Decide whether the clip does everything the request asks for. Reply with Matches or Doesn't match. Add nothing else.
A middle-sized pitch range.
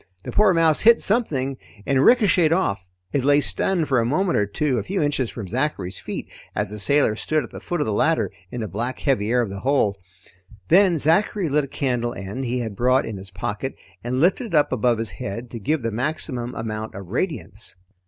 Doesn't match